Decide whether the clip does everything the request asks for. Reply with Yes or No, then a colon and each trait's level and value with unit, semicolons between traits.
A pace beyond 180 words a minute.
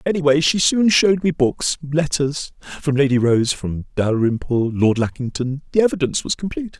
No: average, 140 wpm